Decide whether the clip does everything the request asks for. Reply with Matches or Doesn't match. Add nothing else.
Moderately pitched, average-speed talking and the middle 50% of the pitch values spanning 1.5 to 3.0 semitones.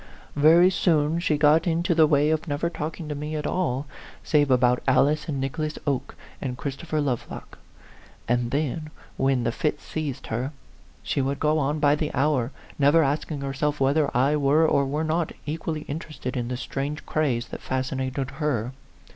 Matches